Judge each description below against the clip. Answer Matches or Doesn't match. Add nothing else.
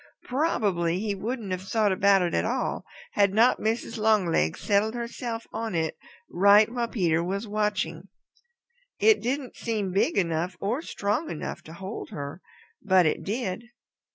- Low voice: Doesn't match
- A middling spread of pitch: Matches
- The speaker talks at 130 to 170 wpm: Matches